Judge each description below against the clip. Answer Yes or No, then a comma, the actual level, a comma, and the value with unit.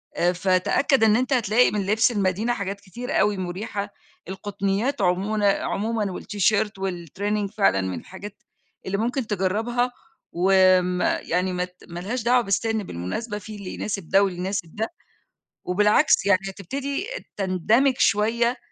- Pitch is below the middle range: No, high, 200 Hz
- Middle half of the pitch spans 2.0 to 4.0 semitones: Yes, average, 3.1 semitones